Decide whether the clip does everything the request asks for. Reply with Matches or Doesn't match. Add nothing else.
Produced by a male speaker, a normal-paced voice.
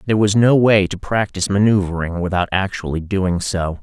Matches